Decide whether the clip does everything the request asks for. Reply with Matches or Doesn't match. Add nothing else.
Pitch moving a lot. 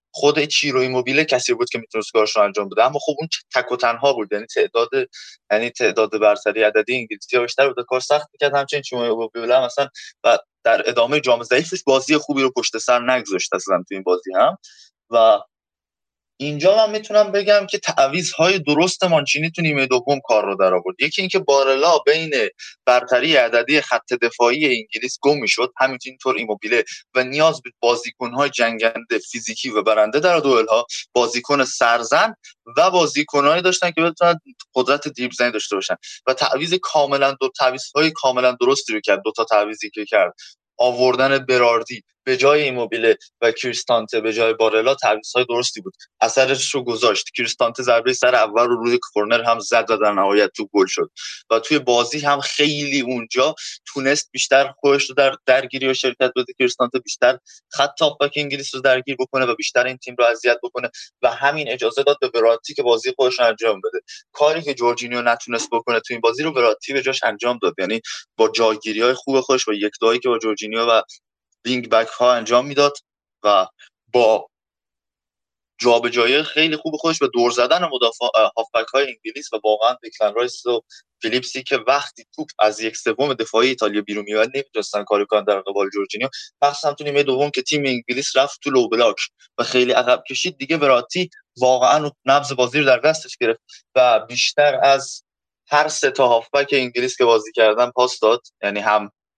Doesn't match